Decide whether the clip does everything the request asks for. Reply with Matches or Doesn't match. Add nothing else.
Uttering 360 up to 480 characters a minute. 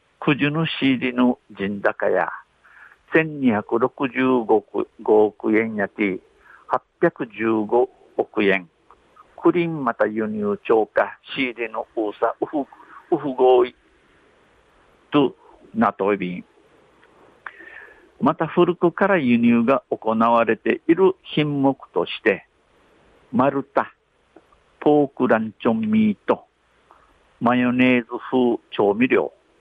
Doesn't match